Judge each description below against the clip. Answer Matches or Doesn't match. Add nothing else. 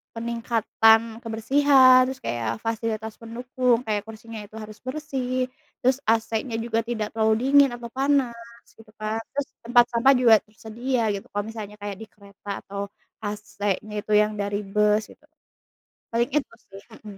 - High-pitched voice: Matches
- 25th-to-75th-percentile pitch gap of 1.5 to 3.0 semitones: Matches